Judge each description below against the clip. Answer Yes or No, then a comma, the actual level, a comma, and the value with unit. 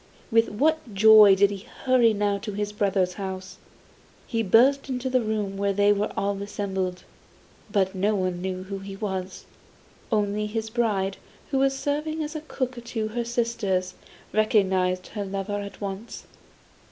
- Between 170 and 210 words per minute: No, average, 155 wpm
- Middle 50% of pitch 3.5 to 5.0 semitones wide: No, average, 3.0 semitones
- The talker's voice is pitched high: Yes, high, 205 Hz